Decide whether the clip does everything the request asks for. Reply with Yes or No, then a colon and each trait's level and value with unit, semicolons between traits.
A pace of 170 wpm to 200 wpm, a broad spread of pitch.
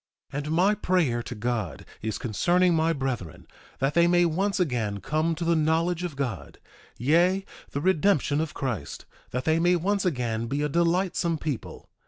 Yes: average, 175 wpm; wide, 5.8 semitones